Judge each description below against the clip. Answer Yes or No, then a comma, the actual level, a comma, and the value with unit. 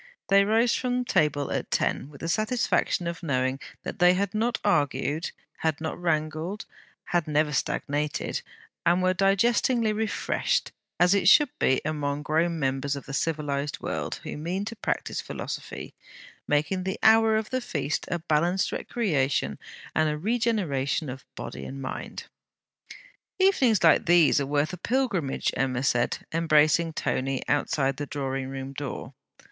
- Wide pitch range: Yes, wide, 5.7 semitones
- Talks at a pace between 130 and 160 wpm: Yes, average, 150 wpm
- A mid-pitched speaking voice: Yes, medium, 160 Hz